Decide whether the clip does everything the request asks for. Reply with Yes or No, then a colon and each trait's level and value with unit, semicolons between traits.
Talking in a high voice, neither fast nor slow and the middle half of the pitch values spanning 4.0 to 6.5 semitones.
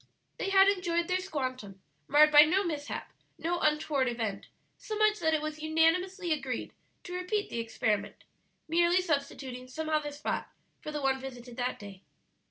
Yes: very high, 305 Hz; average, 165 wpm; average, 5.3 semitones